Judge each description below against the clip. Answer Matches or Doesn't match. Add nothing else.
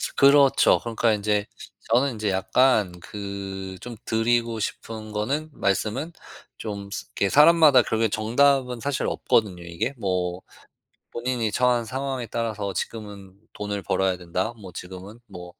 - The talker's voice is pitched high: Doesn't match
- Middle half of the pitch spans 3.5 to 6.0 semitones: Matches